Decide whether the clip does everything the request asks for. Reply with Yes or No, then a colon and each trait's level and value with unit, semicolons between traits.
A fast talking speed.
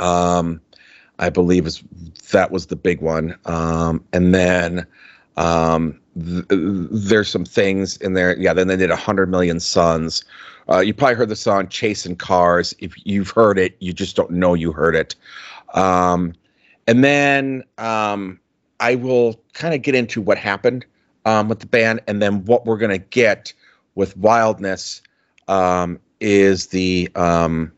No: average, 165 wpm